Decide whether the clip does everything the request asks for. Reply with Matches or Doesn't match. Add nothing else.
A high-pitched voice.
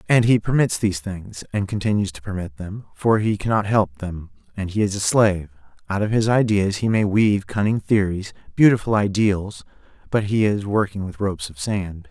Doesn't match